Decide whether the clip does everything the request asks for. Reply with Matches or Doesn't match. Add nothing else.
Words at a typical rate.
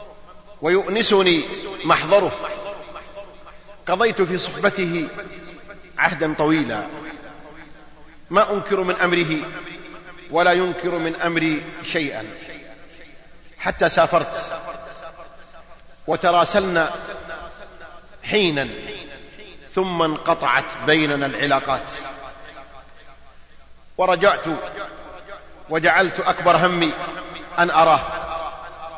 Doesn't match